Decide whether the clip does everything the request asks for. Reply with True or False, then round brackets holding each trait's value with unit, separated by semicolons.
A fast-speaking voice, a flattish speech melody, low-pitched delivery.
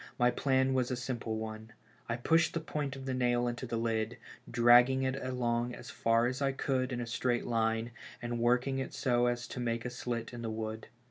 True (215 wpm; 1.8 semitones; 120 Hz)